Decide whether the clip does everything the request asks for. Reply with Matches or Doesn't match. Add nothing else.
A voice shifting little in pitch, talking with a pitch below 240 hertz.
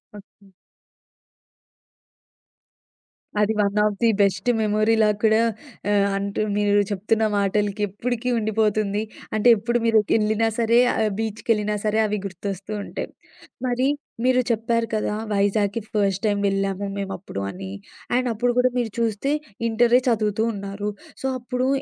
Matches